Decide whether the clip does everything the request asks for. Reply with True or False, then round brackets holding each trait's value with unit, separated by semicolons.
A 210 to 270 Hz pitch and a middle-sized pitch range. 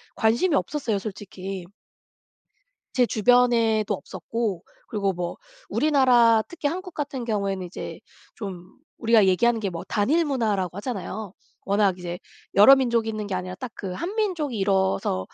True (220 Hz; 4.4 semitones)